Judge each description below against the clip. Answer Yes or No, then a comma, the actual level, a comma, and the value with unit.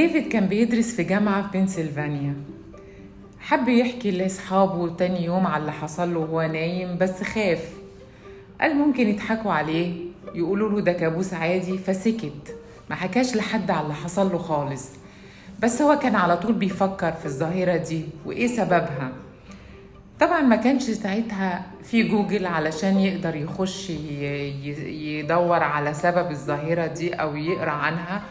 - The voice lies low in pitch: No, medium, 175 Hz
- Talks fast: Yes, fast, 140 wpm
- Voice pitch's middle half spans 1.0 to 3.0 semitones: No, average, 4.6 semitones